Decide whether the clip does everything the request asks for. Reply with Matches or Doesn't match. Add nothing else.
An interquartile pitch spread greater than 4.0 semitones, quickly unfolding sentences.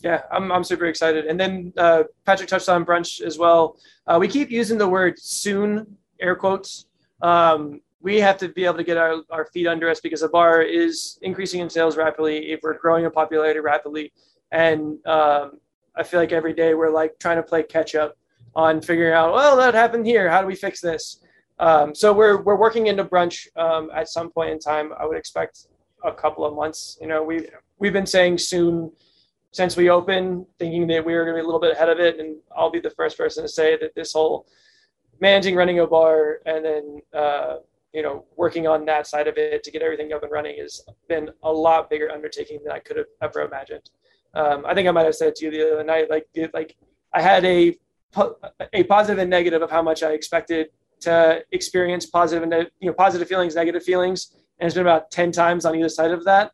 Doesn't match